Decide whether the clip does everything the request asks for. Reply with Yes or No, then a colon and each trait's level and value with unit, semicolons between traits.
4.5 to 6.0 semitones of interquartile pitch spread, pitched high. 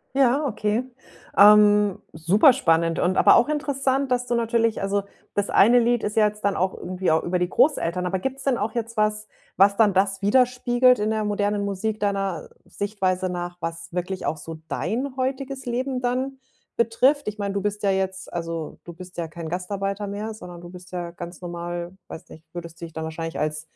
Yes: average, 4.9 semitones; high, 200 Hz